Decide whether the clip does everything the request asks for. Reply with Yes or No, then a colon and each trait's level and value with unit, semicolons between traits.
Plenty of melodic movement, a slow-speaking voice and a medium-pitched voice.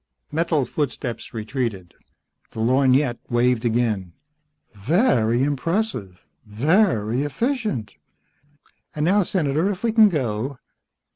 No: wide, 6.7 semitones; slow, 95 wpm; low, 130 Hz